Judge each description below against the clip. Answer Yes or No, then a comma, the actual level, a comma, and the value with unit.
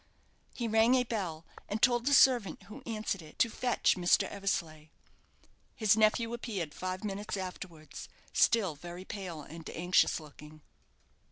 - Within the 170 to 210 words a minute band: No, average, 145 wpm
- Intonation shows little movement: No, average, 5.3 semitones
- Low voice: No, high, 195 Hz